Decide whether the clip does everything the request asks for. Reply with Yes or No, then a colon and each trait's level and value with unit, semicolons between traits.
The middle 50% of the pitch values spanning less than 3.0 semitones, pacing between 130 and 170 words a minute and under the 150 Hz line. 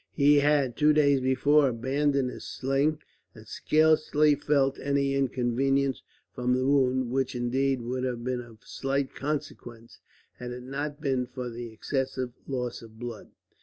Yes: narrow, 2.4 semitones; average, 150 wpm; low, 135 Hz